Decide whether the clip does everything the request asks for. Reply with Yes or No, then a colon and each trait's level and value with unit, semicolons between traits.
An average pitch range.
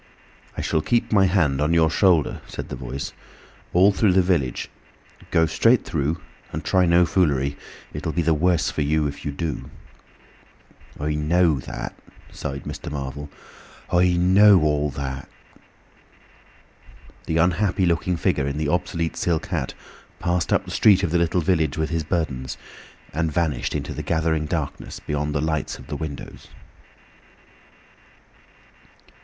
Yes: average, 3.1 semitones